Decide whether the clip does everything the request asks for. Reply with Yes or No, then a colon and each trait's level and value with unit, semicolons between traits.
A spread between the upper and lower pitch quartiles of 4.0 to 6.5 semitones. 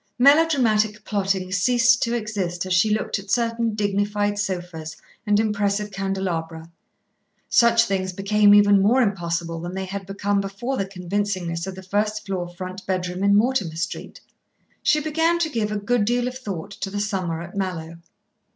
No: average, 2.7 semitones